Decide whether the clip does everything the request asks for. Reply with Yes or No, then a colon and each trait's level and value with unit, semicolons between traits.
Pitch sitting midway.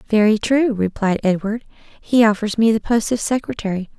No: high, 220 Hz